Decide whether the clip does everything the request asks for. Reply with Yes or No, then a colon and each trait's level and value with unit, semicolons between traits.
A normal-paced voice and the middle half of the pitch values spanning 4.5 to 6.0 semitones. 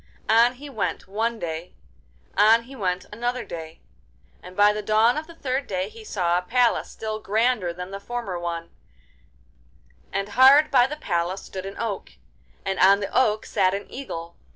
Yes: average, 175 wpm; average, 4.8 semitones